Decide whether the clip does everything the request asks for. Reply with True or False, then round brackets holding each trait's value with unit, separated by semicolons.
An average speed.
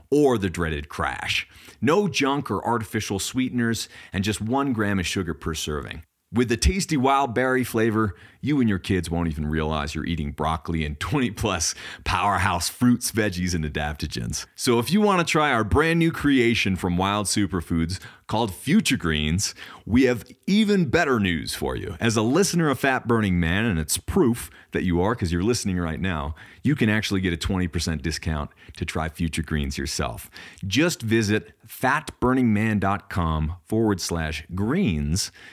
True (170 wpm)